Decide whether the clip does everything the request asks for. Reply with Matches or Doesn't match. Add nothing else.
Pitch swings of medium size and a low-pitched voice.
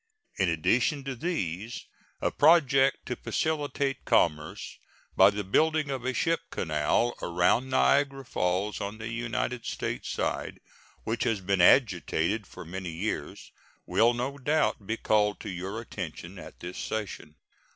Doesn't match